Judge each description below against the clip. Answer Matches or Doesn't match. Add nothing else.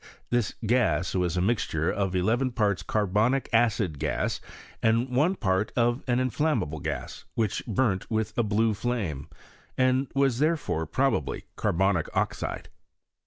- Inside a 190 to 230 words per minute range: Doesn't match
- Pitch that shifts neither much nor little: Matches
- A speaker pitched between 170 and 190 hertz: Doesn't match